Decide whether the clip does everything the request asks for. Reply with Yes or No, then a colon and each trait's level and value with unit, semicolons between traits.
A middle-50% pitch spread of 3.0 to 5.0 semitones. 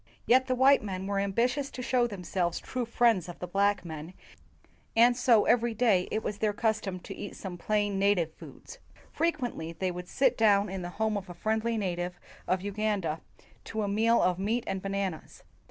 Yes: average, 4.0 semitones